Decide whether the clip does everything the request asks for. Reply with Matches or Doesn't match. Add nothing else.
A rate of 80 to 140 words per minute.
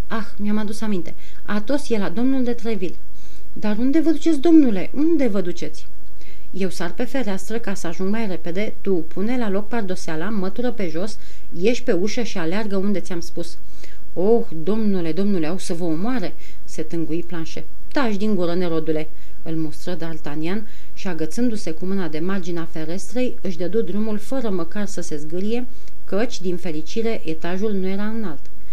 Doesn't match